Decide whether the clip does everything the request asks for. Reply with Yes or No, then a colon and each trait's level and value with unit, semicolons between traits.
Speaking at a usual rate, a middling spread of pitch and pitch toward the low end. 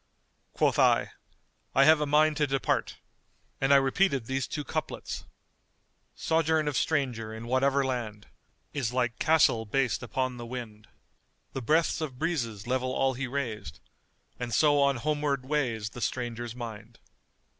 Yes: average, 155 wpm; average, 3.6 semitones; low, 130 Hz